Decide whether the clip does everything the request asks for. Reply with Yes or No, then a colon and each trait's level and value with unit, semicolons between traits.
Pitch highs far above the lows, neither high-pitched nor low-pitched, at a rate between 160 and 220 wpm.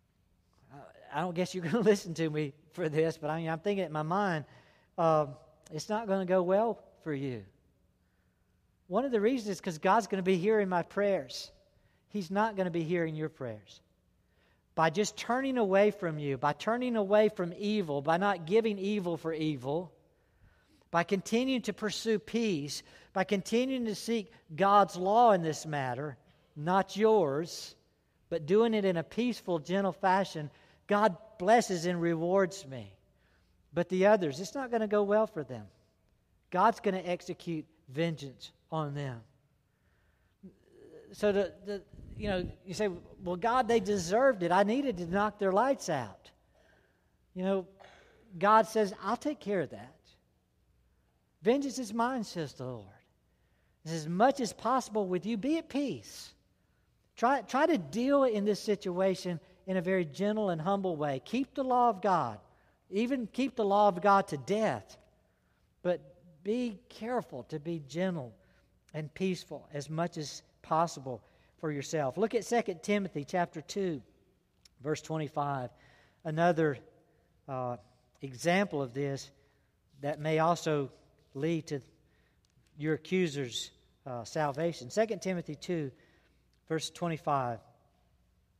No: wide, 5.9 semitones; medium, 175 Hz; average, 150 wpm